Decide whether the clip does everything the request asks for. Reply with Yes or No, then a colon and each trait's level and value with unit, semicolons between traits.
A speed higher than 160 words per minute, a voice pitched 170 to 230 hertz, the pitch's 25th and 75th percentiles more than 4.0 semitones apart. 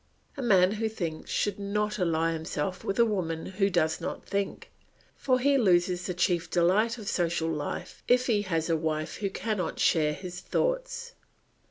Yes: average, 175 wpm; medium, 185 Hz; average, 4.4 semitones